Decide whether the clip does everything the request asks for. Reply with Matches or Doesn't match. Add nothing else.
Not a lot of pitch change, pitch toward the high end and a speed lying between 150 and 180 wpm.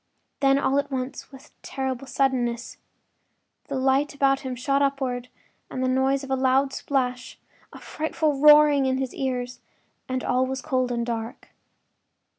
Matches